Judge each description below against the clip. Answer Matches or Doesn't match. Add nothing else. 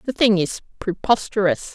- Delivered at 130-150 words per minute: Matches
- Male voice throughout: Doesn't match